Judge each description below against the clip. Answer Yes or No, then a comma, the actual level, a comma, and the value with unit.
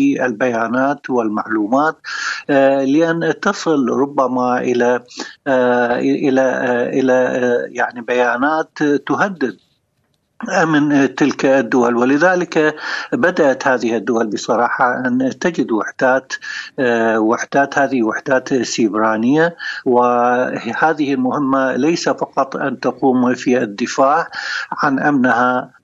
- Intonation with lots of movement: No, average, 3.0 semitones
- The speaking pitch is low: Yes, low, 130 Hz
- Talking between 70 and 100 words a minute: Yes, average, 85 wpm